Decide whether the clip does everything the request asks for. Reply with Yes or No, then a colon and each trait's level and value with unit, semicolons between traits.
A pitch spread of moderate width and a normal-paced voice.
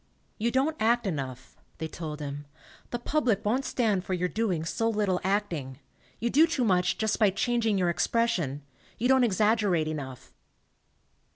No: wide, 6.2 semitones; average, 165 wpm